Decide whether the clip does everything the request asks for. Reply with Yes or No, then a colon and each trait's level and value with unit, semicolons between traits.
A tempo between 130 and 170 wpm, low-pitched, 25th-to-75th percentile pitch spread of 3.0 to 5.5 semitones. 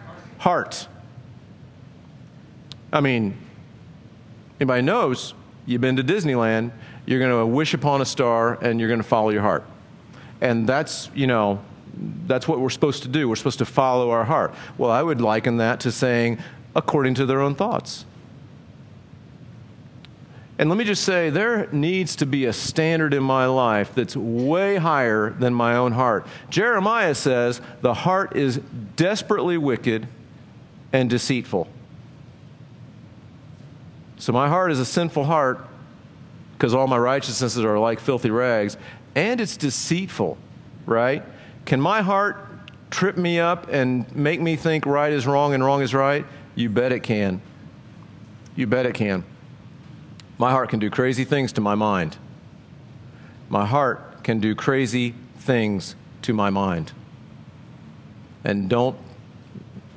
Yes: average, 145 wpm; low, 130 Hz; average, 3.7 semitones